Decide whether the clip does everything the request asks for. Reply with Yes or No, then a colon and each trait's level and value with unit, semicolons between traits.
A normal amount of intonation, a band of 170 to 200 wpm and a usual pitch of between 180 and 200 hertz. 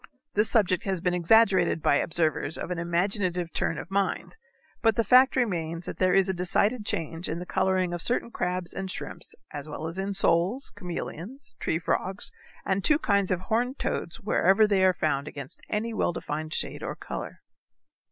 Yes: average, 3.4 semitones; average, 185 wpm; medium, 185 Hz